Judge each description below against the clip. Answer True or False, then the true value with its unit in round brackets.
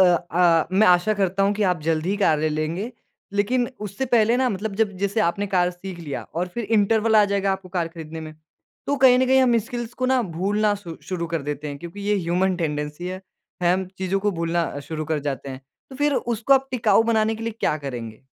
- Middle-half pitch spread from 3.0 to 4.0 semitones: False (4.7 semitones)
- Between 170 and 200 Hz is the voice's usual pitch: True (190 Hz)